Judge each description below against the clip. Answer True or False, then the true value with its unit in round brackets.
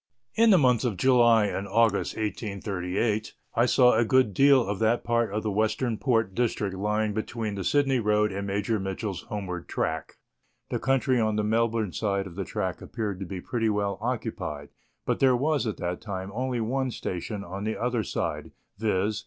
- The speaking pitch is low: True (110 Hz)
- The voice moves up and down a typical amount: True (3.1 semitones)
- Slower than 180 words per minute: False (185 wpm)